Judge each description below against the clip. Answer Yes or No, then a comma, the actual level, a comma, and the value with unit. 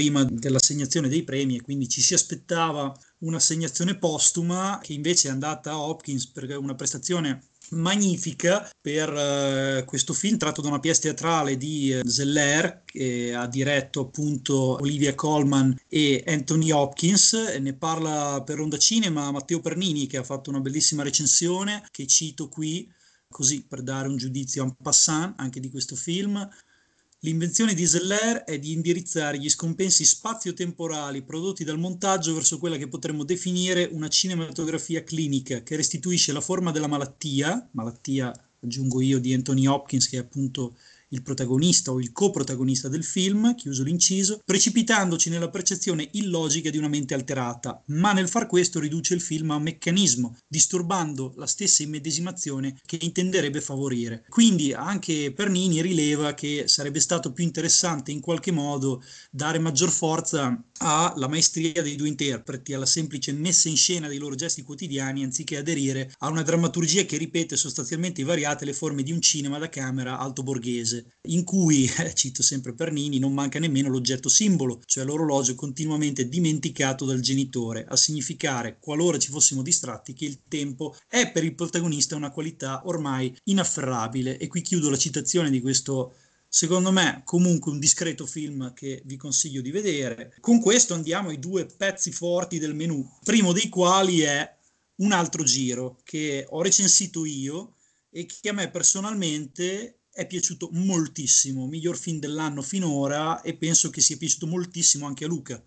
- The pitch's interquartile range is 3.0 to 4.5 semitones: Yes, average, 4.0 semitones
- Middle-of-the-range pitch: Yes, medium, 155 Hz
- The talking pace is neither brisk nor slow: Yes, average, 160 wpm